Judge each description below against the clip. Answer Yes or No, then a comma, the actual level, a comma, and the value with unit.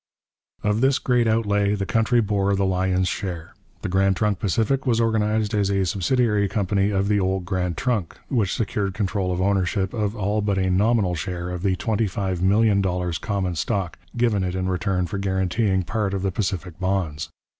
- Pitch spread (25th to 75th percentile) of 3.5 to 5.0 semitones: No, narrow, 2.4 semitones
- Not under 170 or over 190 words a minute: Yes, average, 175 wpm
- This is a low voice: Yes, low, 100 Hz